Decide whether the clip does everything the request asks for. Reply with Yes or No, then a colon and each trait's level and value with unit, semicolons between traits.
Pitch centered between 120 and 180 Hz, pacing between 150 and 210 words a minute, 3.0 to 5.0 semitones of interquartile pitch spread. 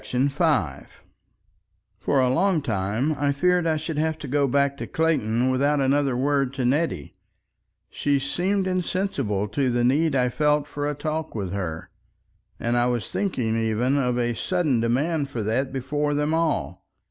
Yes: medium, 140 Hz; average, 170 wpm; average, 4.0 semitones